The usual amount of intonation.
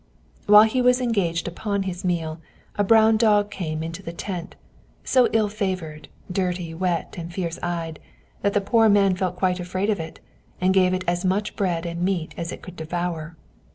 Yes: average, 3.3 semitones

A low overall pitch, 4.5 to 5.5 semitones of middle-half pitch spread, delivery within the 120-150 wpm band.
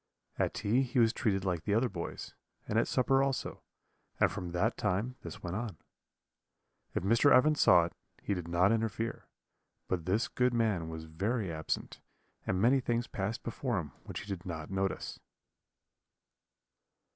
No: low, 105 Hz; average, 5.0 semitones; average, 165 wpm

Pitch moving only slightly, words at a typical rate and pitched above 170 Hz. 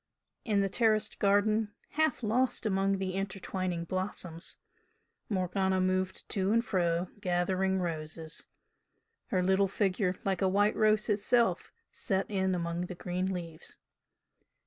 No: narrow, 2.2 semitones; slow, 125 wpm; high, 190 Hz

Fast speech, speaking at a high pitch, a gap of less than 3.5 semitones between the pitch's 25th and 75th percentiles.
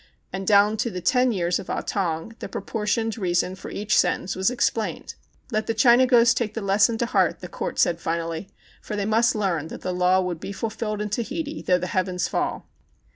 No: fast, 210 wpm; high, 205 Hz; average, 3.8 semitones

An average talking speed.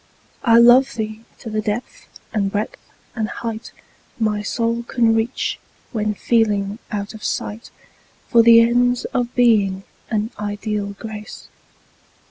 No: slow, 130 wpm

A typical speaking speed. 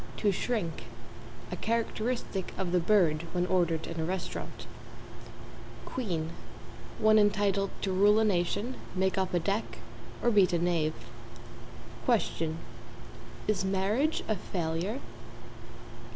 No: slow, 125 wpm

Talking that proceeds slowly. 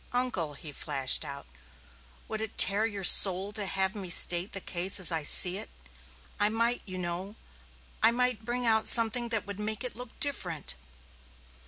No: average, 175 wpm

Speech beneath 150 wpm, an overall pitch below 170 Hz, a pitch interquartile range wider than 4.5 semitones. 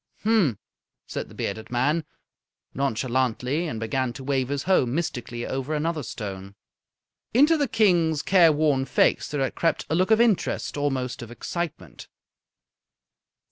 Yes: average, 140 wpm; medium, 140 Hz; average, 5.2 semitones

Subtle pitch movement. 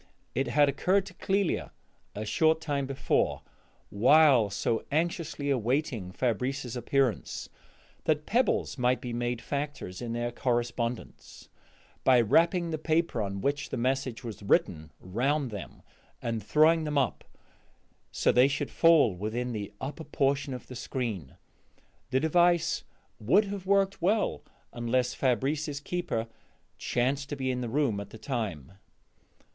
No: average, 4.6 semitones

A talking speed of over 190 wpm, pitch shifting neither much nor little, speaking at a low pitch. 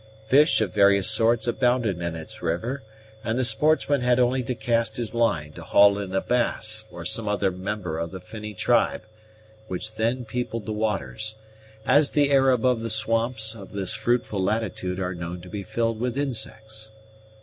No: average, 180 wpm; average, 3.6 semitones; low, 110 Hz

